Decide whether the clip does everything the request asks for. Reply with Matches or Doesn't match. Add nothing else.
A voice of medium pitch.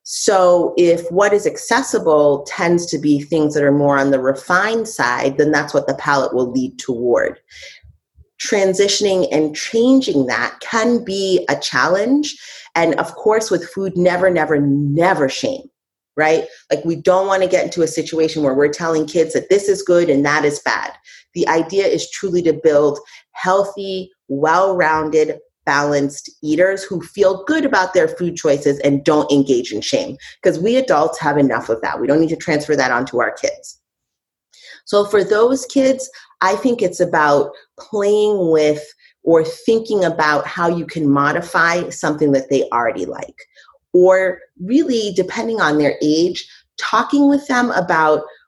Matches